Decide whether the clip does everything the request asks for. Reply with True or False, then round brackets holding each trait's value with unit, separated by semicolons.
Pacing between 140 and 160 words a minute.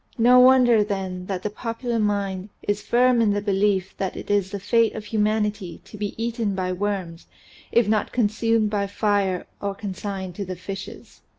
False (180 wpm)